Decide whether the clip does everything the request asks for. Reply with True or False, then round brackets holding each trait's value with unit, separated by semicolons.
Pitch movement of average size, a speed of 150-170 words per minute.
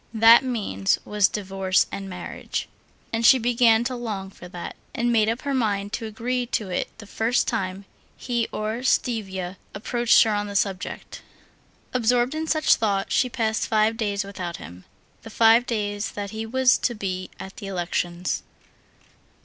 True (3.4 semitones; 165 wpm)